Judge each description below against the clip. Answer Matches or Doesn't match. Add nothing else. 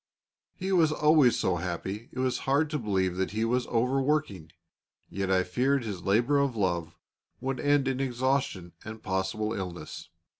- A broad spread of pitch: Matches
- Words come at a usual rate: Matches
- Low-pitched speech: Matches